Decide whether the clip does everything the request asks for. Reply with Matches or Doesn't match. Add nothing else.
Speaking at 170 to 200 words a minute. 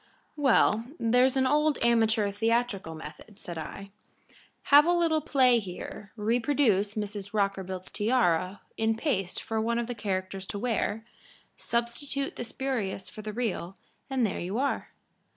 Doesn't match